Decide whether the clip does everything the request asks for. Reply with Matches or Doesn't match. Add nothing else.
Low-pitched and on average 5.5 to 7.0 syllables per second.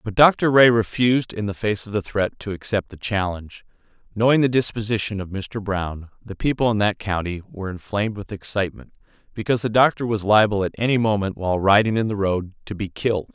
Matches